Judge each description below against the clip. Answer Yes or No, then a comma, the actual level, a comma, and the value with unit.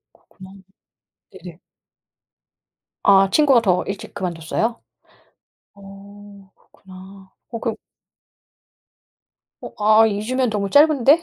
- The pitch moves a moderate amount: Yes, average, 3.0 semitones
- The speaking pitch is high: Yes, high, 205 Hz